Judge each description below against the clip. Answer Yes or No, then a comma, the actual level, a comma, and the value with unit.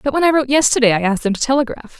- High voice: Yes, very high, 255 Hz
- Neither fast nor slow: No, fast, 300 wpm